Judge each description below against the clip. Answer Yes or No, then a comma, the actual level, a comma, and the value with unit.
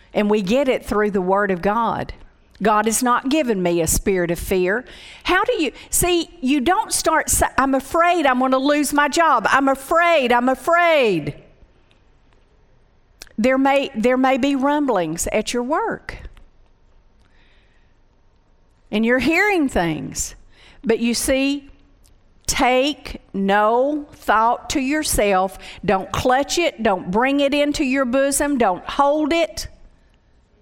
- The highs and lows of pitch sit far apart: Yes, wide, 7.1 semitones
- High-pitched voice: Yes, very high, 255 Hz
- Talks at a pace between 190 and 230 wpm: No, slow, 135 wpm